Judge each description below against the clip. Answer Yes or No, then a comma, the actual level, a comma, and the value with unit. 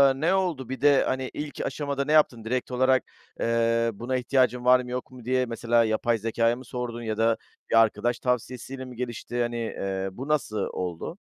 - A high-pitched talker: No, low, 125 Hz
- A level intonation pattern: Yes, narrow, 2.2 semitones